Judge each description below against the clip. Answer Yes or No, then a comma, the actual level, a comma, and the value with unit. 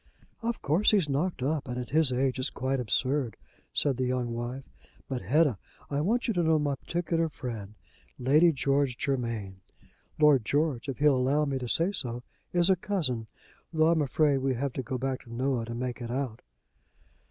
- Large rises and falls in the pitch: No, average, 3.8 semitones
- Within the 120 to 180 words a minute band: No, average, 190 wpm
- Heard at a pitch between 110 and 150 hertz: Yes, low, 135 Hz